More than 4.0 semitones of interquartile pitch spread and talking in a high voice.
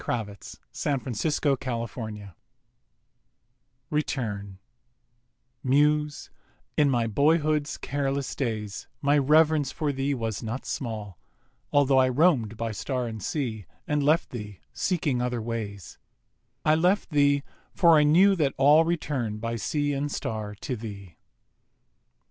No: average, 5.0 semitones; low, 135 Hz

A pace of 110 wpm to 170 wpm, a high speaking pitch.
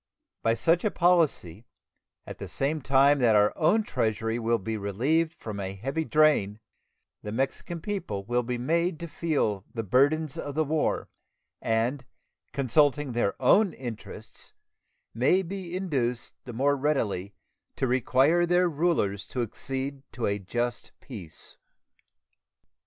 No: average, 140 wpm; low, 135 Hz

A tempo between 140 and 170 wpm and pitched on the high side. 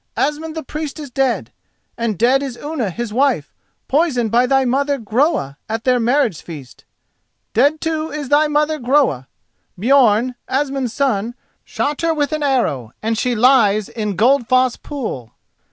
Yes: average, 155 wpm; very high, 255 Hz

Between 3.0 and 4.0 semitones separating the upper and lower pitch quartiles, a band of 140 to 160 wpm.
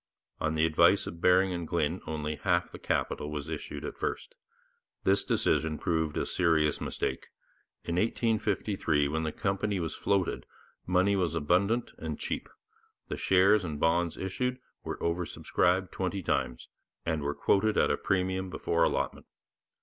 Yes: average, 3.4 semitones; average, 155 wpm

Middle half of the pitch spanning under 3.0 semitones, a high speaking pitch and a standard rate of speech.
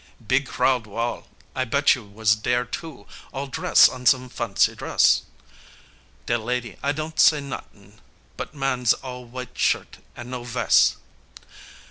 No: narrow, 2.6 semitones; low, 125 Hz; average, 145 wpm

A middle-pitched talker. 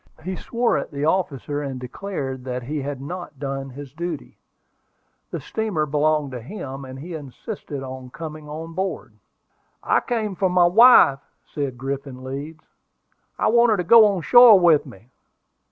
Yes: medium, 150 Hz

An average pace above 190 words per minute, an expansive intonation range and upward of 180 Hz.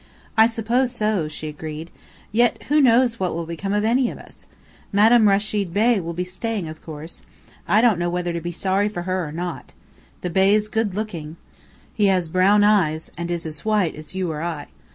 No: average, 200 wpm; average, 4.2 semitones; high, 190 Hz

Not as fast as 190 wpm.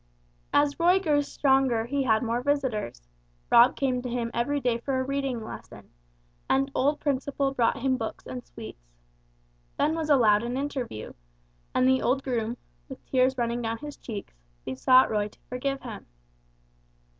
Yes: average, 160 wpm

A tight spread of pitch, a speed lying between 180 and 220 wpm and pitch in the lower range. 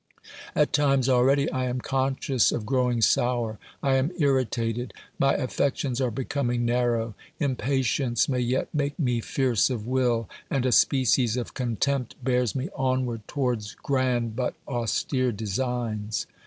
No: narrow, 2.1 semitones; average, 140 wpm; low, 125 Hz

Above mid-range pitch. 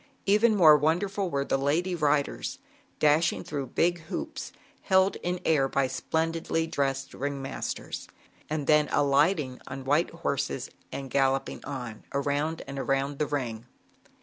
No: medium, 145 Hz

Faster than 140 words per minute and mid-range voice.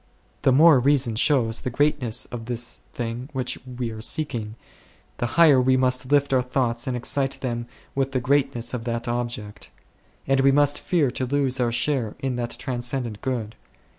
No: average, 180 wpm; low, 125 Hz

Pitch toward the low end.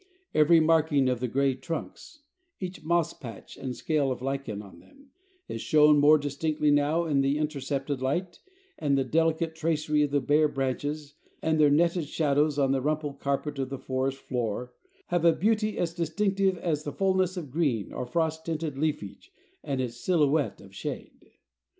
No: medium, 150 Hz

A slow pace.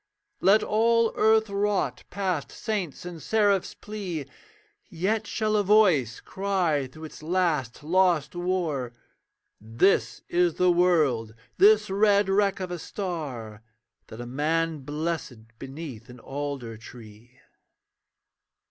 Yes: slow, 120 wpm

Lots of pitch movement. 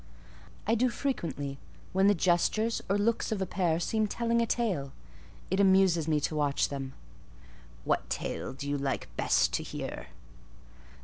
Yes: wide, 7.1 semitones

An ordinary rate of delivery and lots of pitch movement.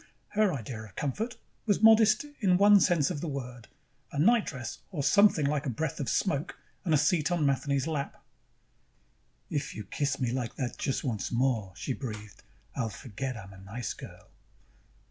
Yes: average, 175 wpm; wide, 6.3 semitones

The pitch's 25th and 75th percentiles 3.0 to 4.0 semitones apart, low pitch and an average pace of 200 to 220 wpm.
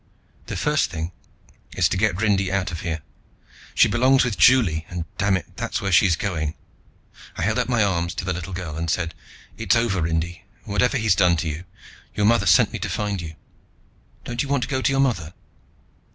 No: average, 4.8 semitones; very low, 95 Hz; fast, 205 wpm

